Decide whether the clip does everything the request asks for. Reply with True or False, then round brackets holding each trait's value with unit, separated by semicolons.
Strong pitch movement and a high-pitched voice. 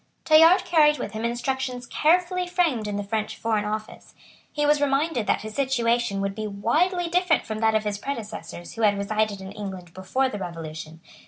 True (6.4 semitones; 225 Hz)